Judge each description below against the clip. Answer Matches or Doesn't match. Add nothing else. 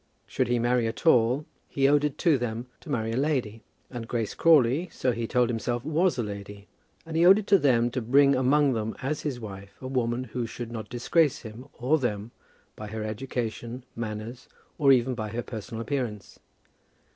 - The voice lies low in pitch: Matches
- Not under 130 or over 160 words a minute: Doesn't match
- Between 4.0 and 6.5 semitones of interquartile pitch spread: Doesn't match